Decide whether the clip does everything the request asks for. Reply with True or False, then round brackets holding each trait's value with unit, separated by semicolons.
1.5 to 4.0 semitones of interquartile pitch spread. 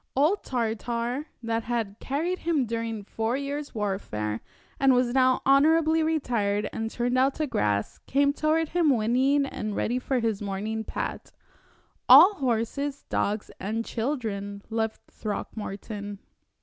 False (4.7 semitones)